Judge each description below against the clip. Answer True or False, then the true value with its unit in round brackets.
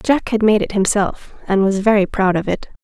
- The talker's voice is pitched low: False (205 Hz)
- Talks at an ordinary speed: False (230 wpm)